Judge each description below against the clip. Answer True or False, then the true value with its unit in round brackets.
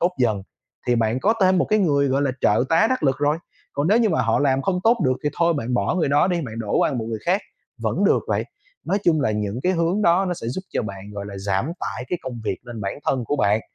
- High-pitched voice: False (140 Hz)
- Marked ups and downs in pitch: True (7.7 semitones)